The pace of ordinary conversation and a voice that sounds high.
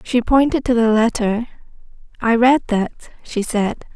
Yes: average, 150 wpm; high, 230 Hz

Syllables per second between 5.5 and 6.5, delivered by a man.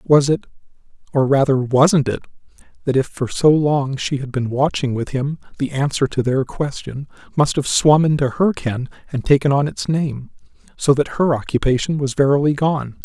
No: 4.9 syllables/s; male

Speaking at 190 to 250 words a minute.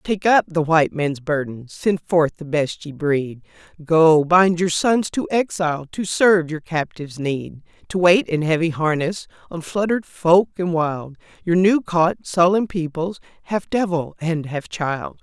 No: average, 170 wpm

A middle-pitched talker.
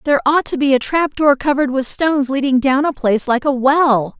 No: very high, 275 Hz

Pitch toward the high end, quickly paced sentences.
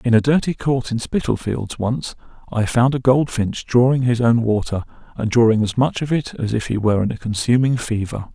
No: low, 120 Hz; fast, 210 wpm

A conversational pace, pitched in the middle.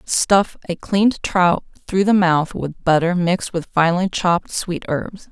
Yes: average, 170 wpm; medium, 180 Hz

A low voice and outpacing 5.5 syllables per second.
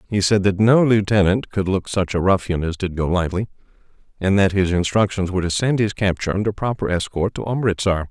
Yes: very low, 95 Hz; 5.9 syllables/s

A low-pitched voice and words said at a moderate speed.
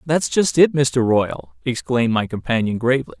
Yes: low, 125 Hz; average, 170 wpm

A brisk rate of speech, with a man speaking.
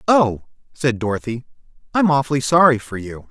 No: average, 145 wpm; male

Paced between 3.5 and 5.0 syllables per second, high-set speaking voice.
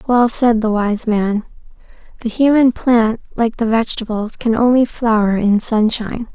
Yes: 4.6 syllables/s; high, 225 Hz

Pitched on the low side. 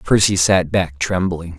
Yes: very low, 90 Hz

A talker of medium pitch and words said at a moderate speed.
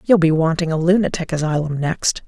Yes: medium, 165 Hz; average, 185 wpm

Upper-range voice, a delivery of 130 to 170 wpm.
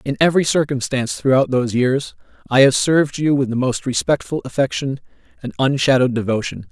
No: low, 135 Hz; average, 160 wpm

